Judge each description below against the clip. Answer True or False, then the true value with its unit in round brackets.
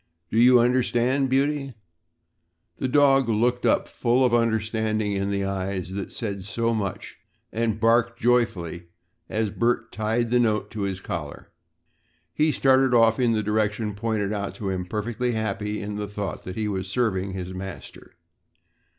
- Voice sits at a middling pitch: False (110 Hz)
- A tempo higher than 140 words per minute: True (160 wpm)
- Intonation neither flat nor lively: True (3.4 semitones)